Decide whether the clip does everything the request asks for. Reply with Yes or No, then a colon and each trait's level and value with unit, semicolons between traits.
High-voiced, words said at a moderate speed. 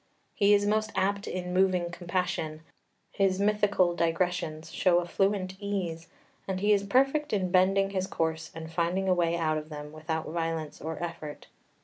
No: medium, 180 Hz; average, 165 wpm